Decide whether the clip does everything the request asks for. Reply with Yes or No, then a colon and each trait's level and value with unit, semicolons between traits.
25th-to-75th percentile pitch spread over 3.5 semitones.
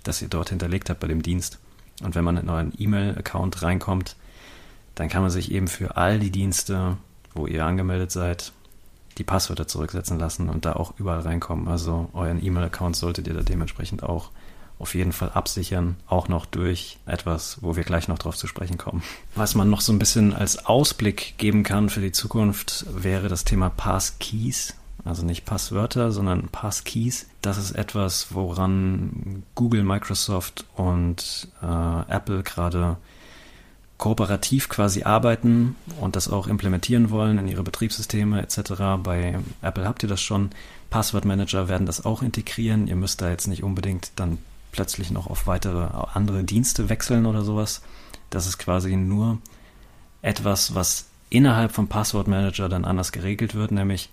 No: average, 2.9 semitones